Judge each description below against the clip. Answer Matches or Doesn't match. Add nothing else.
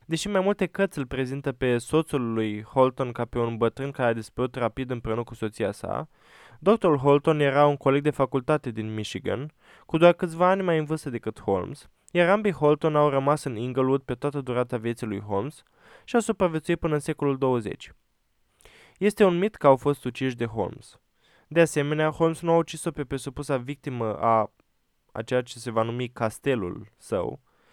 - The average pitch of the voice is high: Doesn't match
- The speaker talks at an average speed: Doesn't match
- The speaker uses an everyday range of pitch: Matches